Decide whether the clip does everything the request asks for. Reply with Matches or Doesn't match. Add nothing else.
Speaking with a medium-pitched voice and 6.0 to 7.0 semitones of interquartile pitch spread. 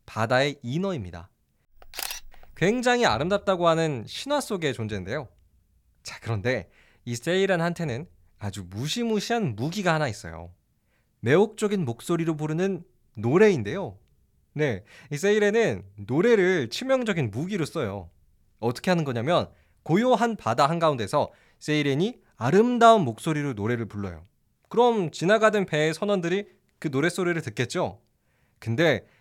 Doesn't match